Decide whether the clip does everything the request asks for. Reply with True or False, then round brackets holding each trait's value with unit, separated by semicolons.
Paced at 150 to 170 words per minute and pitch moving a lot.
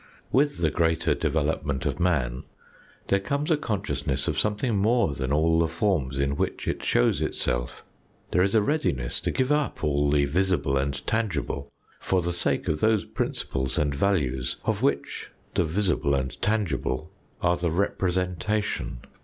True (160 wpm; 6.3 semitones)